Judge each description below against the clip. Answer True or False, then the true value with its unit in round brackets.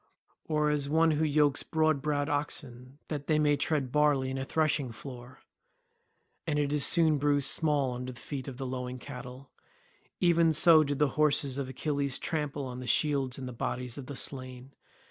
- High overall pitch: False (140 Hz)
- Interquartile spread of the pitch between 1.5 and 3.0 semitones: True (2.6 semitones)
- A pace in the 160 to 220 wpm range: True (175 wpm)